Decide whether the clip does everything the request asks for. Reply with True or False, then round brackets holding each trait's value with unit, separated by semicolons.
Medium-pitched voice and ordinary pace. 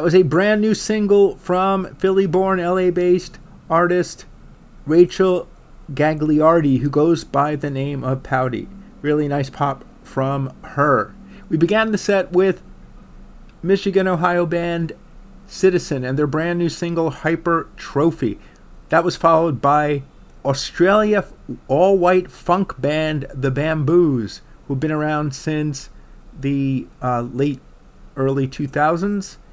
False (165 Hz; 125 wpm)